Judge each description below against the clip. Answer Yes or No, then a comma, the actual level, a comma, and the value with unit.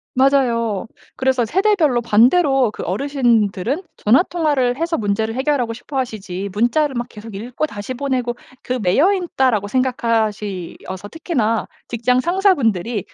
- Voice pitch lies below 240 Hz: No, high, 245 Hz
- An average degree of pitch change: Yes, average, 4.3 semitones